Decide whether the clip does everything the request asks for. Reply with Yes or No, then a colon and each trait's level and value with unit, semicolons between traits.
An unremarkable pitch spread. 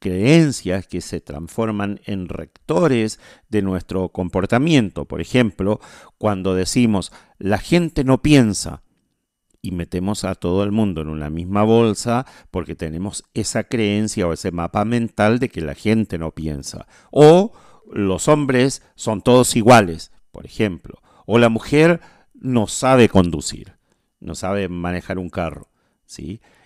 Yes: average, 4.9 semitones